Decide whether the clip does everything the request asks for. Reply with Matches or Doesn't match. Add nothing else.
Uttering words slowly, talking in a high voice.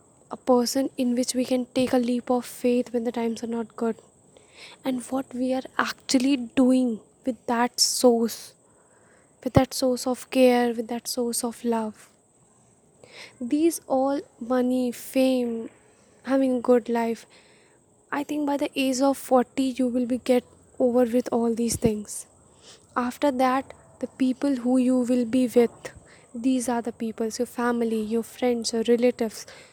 Doesn't match